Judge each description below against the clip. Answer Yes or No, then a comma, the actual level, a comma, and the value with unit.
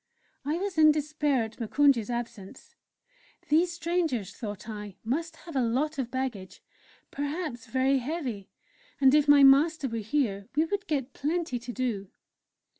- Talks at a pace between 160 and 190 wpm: No, average, 150 wpm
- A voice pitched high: Yes, very high, 270 Hz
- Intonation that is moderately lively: Yes, average, 5.0 semitones